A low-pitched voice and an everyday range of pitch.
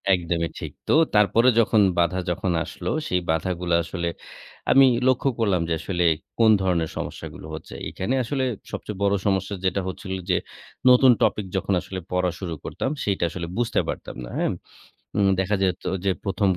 Yes: very low, 95 Hz; average, 3.0 semitones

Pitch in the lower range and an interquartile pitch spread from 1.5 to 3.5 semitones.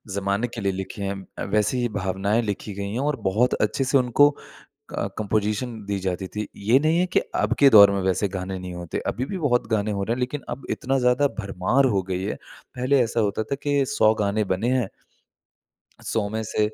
No: low, 110 Hz; average, 4.0 semitones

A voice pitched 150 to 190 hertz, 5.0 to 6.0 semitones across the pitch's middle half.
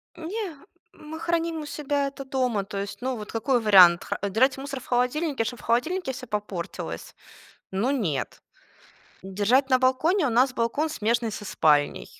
No: very high, 255 Hz; wide, 5.4 semitones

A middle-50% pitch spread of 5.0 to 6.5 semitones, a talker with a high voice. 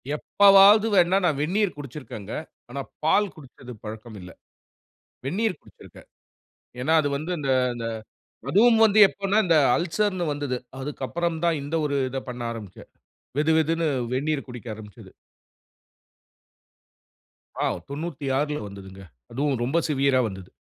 No: average, 5.3 semitones; medium, 145 Hz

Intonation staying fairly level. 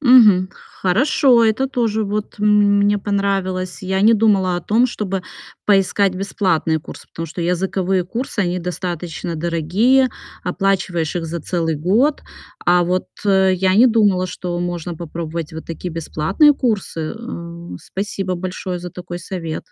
No: average, 3.1 semitones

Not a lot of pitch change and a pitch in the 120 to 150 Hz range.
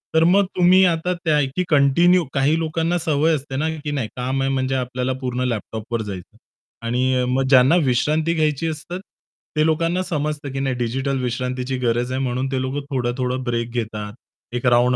No: average, 4.0 semitones; low, 135 Hz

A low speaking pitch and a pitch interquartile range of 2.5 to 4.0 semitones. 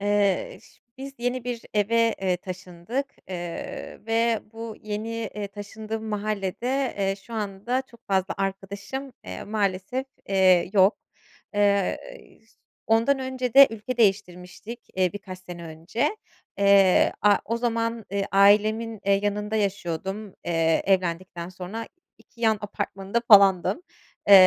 No: high, 205 Hz; average, 3.2 semitones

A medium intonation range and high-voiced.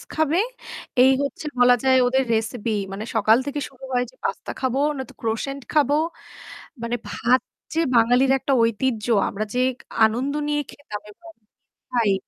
Yes: average, 3.2 semitones; very high, 250 Hz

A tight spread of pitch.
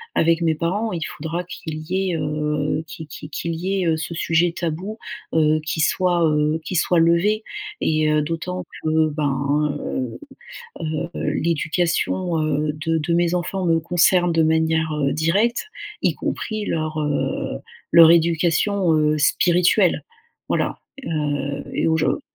Yes: narrow, 2.3 semitones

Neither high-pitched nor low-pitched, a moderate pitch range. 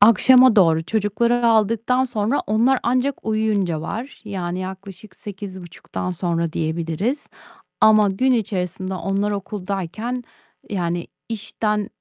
No: high, 205 Hz; average, 3.9 semitones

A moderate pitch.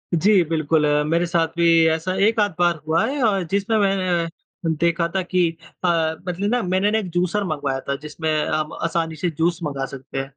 Yes: medium, 170 Hz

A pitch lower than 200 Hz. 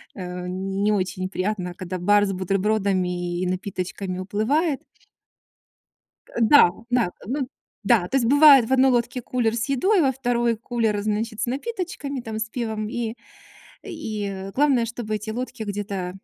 No: high, 220 Hz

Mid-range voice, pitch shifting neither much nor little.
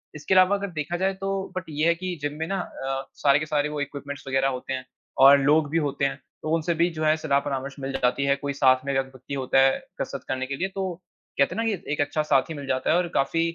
Yes: medium, 145 Hz; average, 3.5 semitones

